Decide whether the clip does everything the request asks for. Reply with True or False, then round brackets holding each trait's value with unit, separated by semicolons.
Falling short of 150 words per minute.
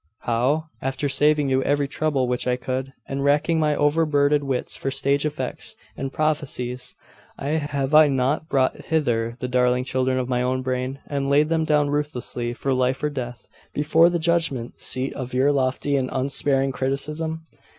False (170 wpm)